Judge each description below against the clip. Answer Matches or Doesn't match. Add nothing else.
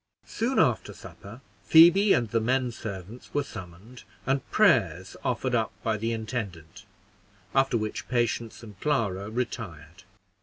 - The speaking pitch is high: Doesn't match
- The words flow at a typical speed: Doesn't match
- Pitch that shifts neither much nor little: Matches